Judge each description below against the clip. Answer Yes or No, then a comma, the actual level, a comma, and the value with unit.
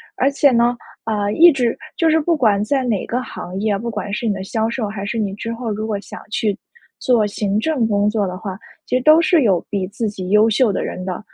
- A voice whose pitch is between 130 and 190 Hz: No, high, 220 Hz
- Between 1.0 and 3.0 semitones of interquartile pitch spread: No, average, 3.5 semitones